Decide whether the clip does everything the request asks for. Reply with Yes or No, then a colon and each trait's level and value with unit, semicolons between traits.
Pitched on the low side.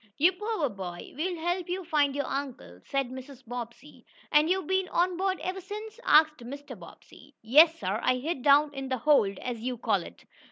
No: very high, 285 Hz